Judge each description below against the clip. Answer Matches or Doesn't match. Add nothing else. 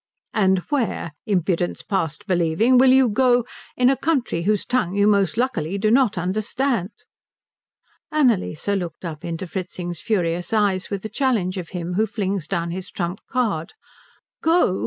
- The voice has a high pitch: Matches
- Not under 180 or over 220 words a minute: Doesn't match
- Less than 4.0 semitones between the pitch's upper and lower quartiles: Doesn't match